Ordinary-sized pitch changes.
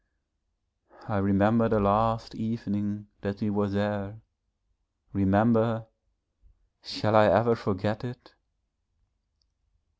No: narrow, 1.9 semitones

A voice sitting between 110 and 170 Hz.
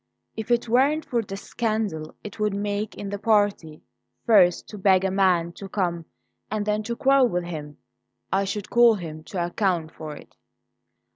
No: high, 200 Hz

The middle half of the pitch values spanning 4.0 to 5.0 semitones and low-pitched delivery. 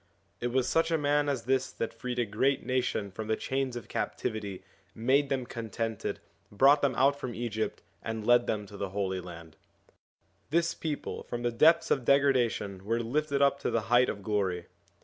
Yes: average, 4.3 semitones; low, 120 Hz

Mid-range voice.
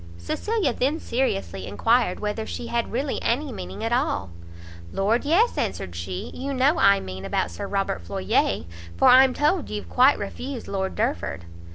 No: high, 230 Hz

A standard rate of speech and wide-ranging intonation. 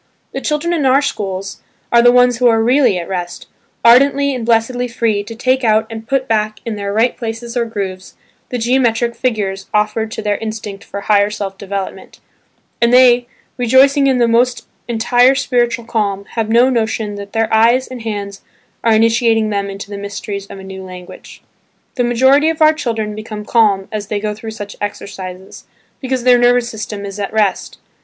No: average, 185 wpm; average, 3.2 semitones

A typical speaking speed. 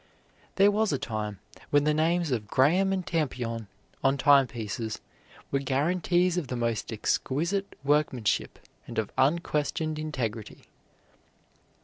No: slow, 120 wpm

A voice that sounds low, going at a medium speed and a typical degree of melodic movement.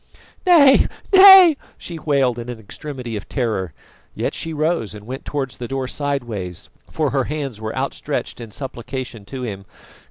Yes: low, 130 Hz; average, 160 wpm; average, 5.0 semitones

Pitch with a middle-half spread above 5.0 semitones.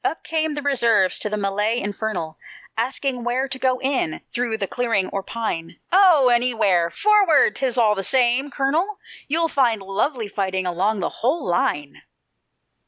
Yes: wide, 5.5 semitones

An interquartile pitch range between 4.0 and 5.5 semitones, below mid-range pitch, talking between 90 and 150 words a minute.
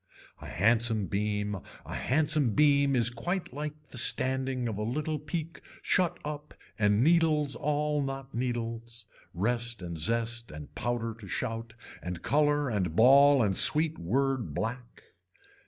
Yes: average, 4.7 semitones; low, 125 Hz; average, 140 wpm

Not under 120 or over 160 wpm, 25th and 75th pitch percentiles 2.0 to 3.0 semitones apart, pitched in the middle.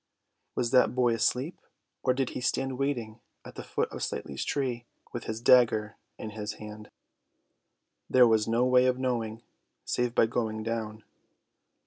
No: average, 155 wpm; narrow, 2.5 semitones; low, 120 Hz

